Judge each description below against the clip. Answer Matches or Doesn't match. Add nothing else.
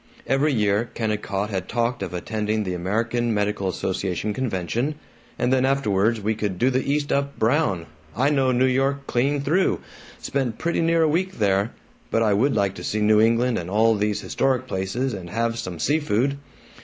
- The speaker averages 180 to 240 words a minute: Matches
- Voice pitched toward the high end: Doesn't match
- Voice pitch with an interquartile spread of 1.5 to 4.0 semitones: Doesn't match